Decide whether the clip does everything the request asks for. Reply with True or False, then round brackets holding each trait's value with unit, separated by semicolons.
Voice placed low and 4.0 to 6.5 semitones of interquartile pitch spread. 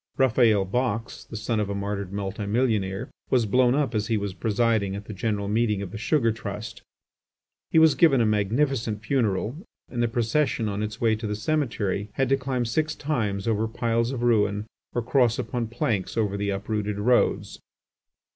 False (110 Hz; 3.0 semitones)